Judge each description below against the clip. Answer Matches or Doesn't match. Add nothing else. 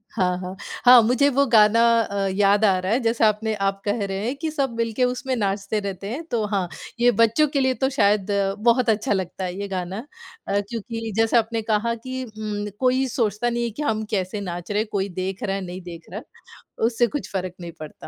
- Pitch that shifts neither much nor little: Matches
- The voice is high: Matches